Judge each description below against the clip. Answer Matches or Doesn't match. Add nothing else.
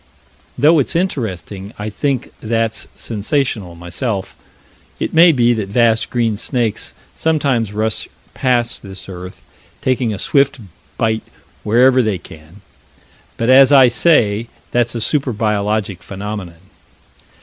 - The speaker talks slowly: Matches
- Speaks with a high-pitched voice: Doesn't match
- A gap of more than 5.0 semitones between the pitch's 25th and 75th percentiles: Doesn't match